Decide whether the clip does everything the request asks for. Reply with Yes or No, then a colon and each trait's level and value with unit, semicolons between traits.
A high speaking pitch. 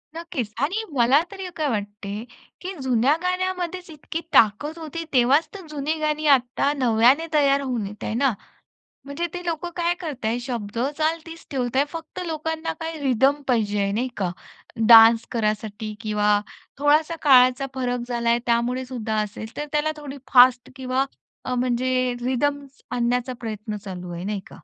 Yes: very high, 255 Hz